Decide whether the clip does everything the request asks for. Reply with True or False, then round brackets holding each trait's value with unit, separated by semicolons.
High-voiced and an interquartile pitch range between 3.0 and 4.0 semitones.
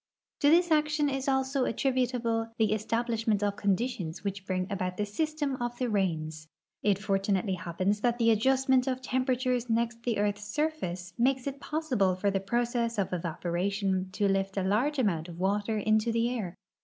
False (220 Hz; 4.7 semitones)